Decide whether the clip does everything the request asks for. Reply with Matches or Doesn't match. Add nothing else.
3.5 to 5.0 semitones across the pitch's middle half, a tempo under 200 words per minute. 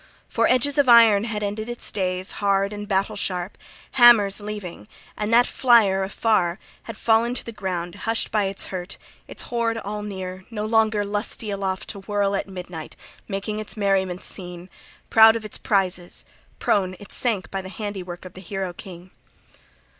Doesn't match